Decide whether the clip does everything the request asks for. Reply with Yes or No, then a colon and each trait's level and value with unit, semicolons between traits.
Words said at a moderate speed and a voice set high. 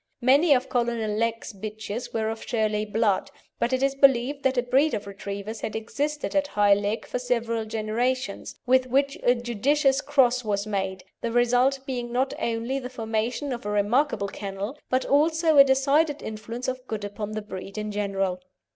Yes: average, 180 wpm; high, 235 Hz